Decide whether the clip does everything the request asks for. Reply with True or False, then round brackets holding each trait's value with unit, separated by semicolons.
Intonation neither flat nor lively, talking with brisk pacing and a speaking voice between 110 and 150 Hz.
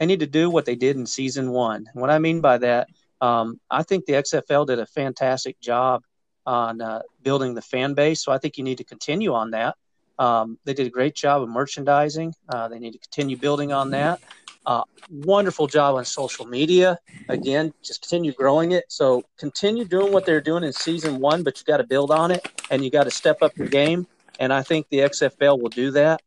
True (3.4 semitones; 225 wpm; 140 Hz)